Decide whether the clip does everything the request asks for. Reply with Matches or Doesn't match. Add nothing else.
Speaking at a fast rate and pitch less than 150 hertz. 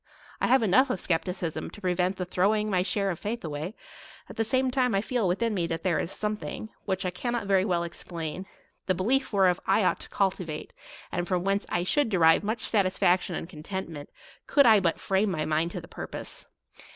Doesn't match